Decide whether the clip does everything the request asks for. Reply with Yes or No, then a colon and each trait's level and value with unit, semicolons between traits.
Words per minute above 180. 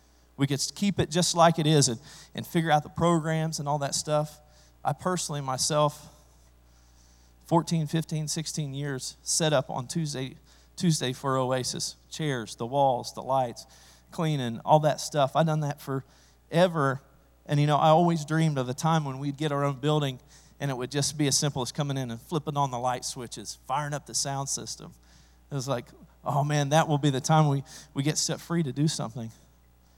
Yes: average, 200 wpm